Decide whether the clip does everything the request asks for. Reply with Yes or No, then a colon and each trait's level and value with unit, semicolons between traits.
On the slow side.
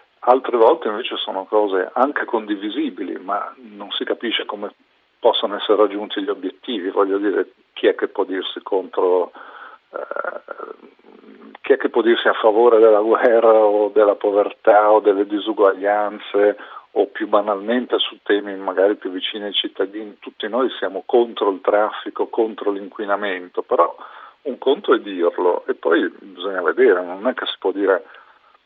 No: average, 155 wpm